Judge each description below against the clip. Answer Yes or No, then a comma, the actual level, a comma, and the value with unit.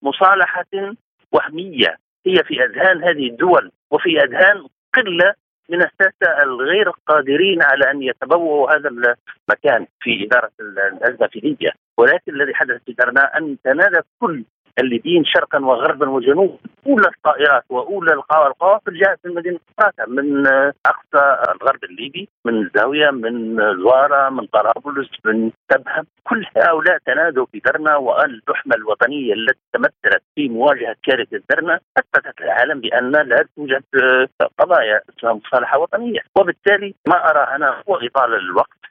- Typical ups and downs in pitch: No, wide, 6.4 semitones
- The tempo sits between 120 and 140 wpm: Yes, average, 130 wpm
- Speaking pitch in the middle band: Yes, medium, 155 Hz